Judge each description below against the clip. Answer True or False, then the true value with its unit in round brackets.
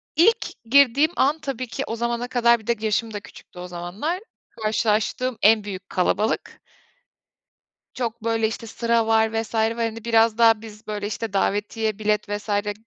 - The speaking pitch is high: True (225 Hz)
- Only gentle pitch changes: True (1.9 semitones)